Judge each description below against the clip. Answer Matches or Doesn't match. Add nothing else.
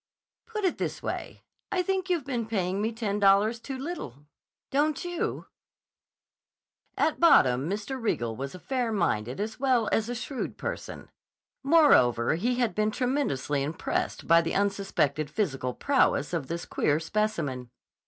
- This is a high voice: Matches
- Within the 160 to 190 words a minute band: Doesn't match